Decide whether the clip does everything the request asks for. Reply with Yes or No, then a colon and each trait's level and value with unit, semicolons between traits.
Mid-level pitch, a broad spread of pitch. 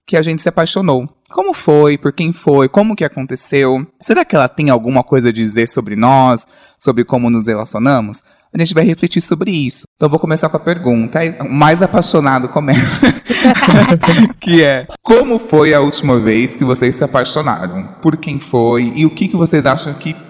No: medium, 150 Hz; average, 4.8 semitones